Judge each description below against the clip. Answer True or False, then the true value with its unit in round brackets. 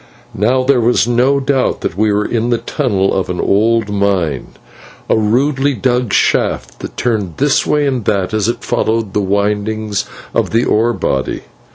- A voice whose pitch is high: False (110 Hz)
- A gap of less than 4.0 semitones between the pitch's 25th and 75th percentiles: True (3.4 semitones)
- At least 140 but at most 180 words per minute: True (175 wpm)